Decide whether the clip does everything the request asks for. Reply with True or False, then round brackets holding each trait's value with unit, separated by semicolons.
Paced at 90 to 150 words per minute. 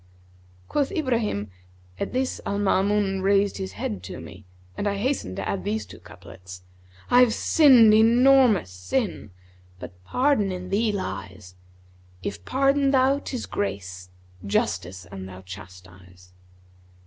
True (135 wpm)